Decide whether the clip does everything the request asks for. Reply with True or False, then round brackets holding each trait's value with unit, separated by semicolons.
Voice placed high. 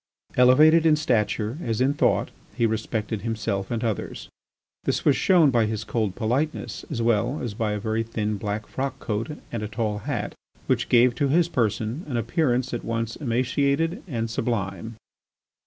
False (115 Hz)